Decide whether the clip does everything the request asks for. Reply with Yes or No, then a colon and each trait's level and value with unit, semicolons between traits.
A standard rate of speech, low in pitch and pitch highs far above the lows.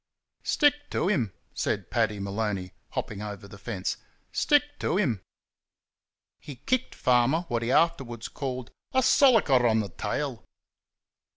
No: slow, 130 wpm; low, 120 Hz; wide, 8.2 semitones